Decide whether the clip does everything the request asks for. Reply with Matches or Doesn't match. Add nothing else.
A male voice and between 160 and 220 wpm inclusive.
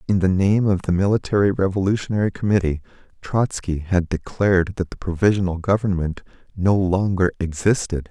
Doesn't match